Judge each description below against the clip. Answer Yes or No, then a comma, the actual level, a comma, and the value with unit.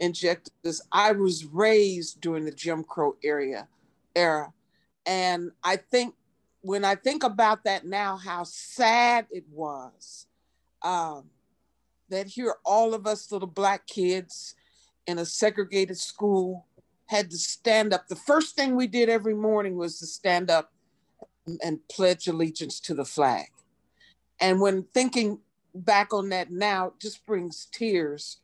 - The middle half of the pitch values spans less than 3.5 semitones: No, average, 4.0 semitones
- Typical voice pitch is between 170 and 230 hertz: Yes, medium, 185 Hz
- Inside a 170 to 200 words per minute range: No, average, 145 wpm